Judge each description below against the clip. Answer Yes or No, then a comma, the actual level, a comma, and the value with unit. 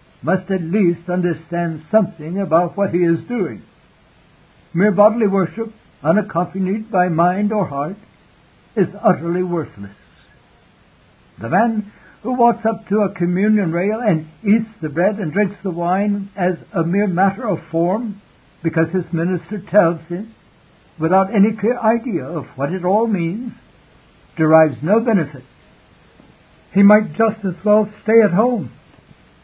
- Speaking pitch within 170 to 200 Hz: Yes, high, 190 Hz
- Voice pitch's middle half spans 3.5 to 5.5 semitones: Yes, average, 3.9 semitones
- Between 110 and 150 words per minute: Yes, average, 140 wpm